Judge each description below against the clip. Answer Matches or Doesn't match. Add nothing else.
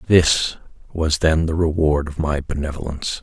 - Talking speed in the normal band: Matches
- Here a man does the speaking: Matches